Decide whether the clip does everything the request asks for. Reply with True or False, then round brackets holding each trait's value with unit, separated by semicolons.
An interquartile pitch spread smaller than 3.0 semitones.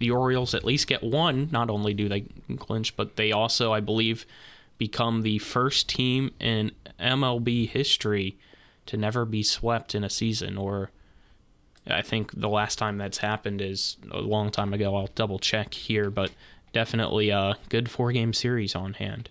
True (2.6 semitones)